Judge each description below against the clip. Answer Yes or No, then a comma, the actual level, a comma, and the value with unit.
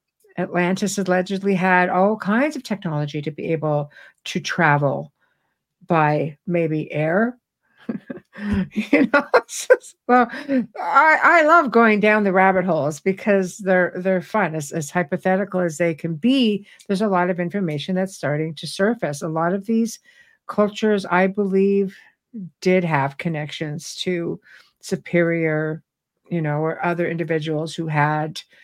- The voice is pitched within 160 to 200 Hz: Yes, medium, 185 Hz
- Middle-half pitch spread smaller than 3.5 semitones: No, average, 4.3 semitones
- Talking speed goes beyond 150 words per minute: No, average, 140 wpm